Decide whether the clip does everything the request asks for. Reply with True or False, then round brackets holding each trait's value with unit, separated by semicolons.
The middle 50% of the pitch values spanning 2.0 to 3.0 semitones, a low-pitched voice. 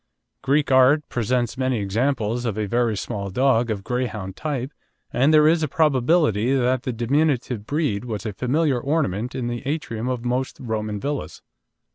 False (3.7 semitones; 125 Hz)